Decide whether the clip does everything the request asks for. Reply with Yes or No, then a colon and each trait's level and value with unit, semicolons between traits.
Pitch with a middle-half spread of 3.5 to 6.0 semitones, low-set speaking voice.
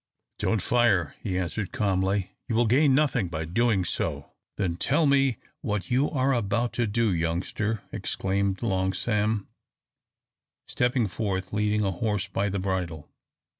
Yes: average, 4.1 semitones; low, 105 Hz